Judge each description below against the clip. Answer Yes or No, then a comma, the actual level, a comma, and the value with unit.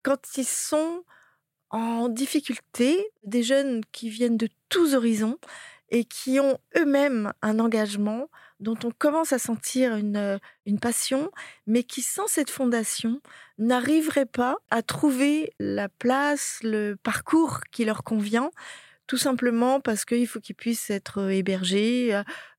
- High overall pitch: Yes, high, 240 Hz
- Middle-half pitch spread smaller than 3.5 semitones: No, average, 3.8 semitones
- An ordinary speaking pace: No, slow, 135 wpm